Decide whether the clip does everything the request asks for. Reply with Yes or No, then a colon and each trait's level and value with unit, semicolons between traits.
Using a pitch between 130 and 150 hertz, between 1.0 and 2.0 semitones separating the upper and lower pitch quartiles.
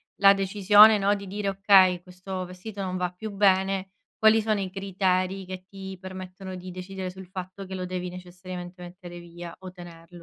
No: medium, 185 Hz; narrow, 1.4 semitones